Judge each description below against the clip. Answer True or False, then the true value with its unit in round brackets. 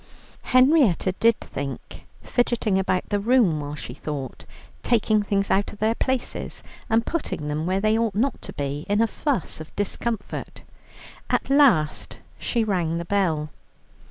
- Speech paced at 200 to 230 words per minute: False (155 wpm)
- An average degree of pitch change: False (6.2 semitones)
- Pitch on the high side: True (205 Hz)